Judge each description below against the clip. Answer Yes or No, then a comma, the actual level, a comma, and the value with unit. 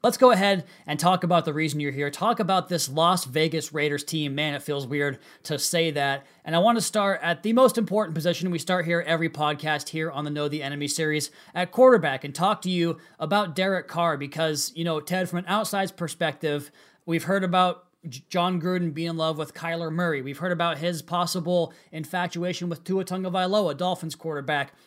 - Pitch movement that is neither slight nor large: Yes, average, 3.0 semitones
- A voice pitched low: No, medium, 170 Hz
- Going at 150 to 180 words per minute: No, fast, 205 wpm